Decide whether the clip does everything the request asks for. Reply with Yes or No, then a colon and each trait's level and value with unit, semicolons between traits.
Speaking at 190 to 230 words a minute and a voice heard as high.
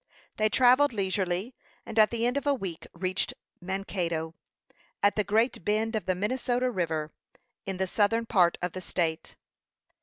No: average, 160 wpm; high, 200 Hz